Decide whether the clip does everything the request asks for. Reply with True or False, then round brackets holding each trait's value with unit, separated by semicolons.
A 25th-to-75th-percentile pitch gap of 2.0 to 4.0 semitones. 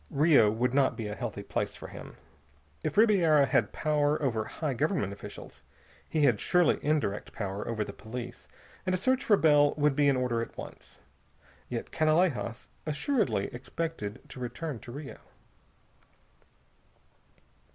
False (5.3 semitones)